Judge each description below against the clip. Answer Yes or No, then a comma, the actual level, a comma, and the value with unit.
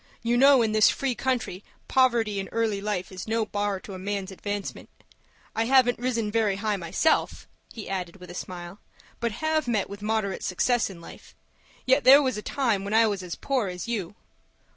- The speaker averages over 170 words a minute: Yes, average, 195 wpm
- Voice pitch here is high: Yes, high, 215 Hz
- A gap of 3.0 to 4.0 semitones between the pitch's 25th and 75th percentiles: Yes, average, 3.7 semitones